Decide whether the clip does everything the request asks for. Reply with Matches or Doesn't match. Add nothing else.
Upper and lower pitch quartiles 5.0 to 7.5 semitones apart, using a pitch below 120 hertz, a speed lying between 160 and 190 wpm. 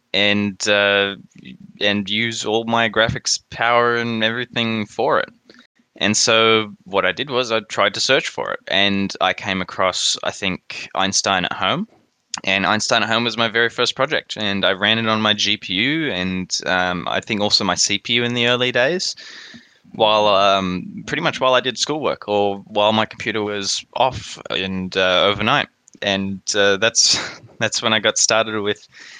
Doesn't match